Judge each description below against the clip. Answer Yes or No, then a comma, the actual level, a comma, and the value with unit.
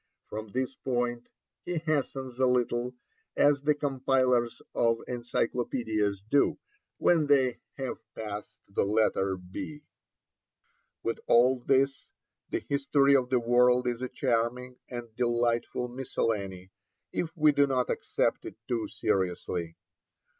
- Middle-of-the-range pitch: No, low, 125 Hz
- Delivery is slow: Yes, slow, 125 wpm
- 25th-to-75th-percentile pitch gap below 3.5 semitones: Yes, narrow, 2.6 semitones